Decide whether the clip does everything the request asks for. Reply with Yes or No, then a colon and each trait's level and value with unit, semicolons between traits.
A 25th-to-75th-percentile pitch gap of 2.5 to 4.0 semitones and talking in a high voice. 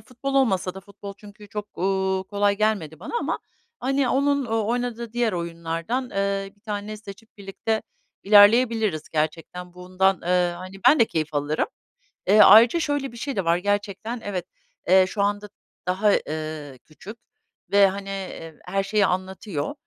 Yes: average, 3.3 semitones; high, 200 Hz